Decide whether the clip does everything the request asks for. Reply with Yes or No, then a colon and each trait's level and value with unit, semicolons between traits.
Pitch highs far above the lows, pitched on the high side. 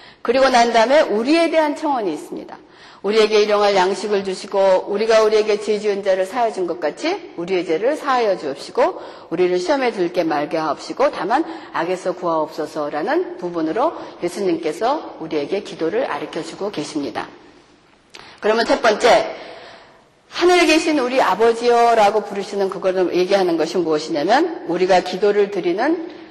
Yes: wide, 7.6 semitones; high, 205 Hz